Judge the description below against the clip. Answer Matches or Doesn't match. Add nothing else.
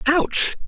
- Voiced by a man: Matches